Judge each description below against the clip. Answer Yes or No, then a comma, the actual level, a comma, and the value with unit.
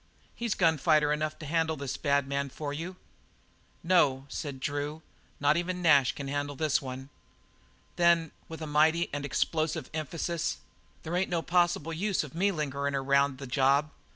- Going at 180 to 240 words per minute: No, average, 165 wpm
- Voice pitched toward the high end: No, medium, 150 Hz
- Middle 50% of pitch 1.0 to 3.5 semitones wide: Yes, average, 2.9 semitones